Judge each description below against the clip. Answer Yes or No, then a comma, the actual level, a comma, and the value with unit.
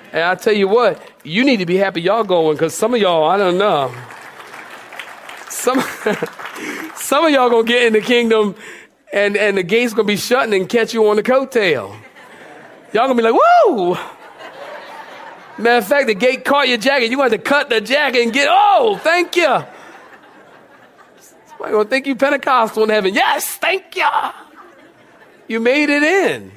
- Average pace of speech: Yes, average, 185 wpm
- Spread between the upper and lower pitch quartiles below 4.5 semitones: No, average, 4.9 semitones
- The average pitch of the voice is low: No, high, 240 Hz